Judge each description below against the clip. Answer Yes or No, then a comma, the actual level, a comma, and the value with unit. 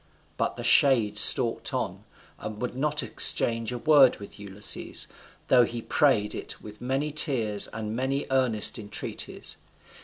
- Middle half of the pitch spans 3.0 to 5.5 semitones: Yes, average, 4.0 semitones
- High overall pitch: No, low, 120 Hz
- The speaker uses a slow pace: No, average, 145 wpm